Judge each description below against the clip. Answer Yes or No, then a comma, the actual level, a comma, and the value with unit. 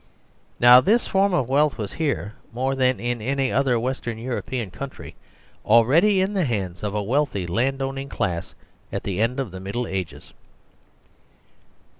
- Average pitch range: Yes, average, 4.4 semitones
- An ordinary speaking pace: Yes, average, 160 wpm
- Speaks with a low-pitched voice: Yes, low, 125 Hz